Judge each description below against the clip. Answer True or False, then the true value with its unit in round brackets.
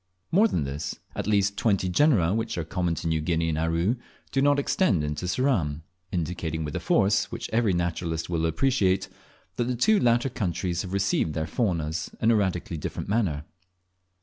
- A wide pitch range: True (5.8 semitones)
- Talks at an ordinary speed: True (180 wpm)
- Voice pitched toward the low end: True (90 Hz)